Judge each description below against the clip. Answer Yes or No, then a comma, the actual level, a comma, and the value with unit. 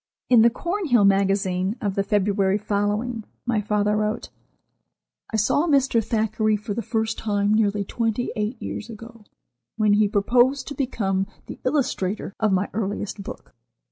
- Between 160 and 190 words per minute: No, average, 150 wpm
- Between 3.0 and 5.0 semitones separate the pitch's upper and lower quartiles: No, narrow, 2.4 semitones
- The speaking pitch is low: No, high, 215 Hz